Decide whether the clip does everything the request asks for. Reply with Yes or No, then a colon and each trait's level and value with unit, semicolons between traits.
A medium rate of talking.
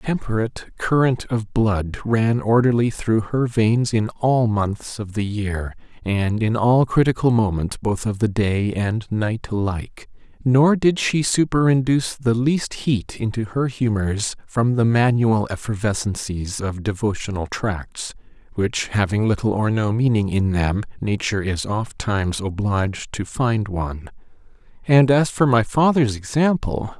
Yes: average, 145 wpm